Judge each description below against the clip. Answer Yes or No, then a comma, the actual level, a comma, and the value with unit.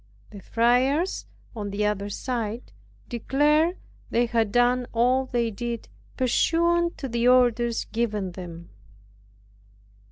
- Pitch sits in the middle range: No, high, 240 Hz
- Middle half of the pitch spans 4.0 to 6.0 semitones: No, average, 3.0 semitones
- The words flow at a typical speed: No, slow, 115 wpm